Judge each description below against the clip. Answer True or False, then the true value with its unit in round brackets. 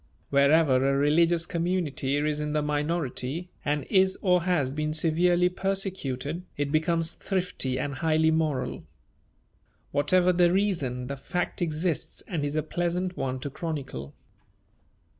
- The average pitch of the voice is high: False (155 Hz)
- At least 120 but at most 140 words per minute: True (135 wpm)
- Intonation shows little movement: False (3.8 semitones)